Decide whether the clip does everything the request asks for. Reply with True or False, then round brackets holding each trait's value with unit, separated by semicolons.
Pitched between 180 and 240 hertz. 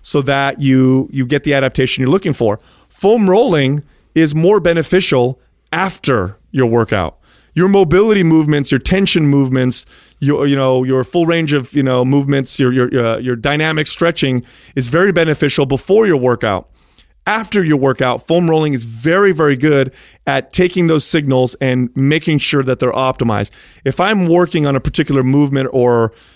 False (140 Hz)